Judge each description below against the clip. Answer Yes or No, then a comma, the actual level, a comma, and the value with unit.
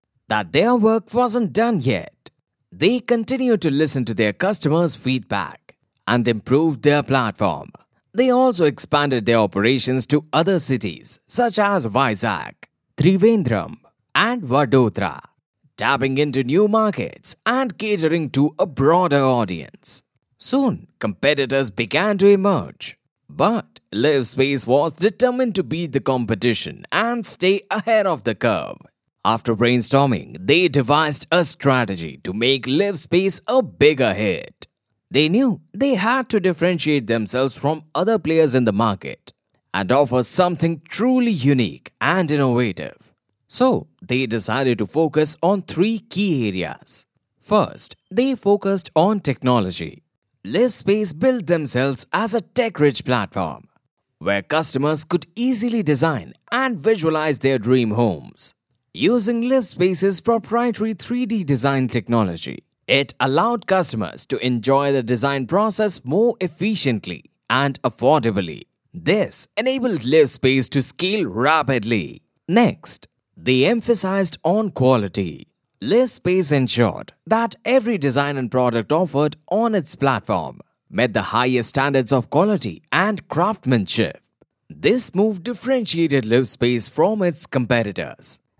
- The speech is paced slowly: Yes, slow, 120 wpm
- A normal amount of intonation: No, wide, 8.5 semitones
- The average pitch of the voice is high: No, medium, 150 Hz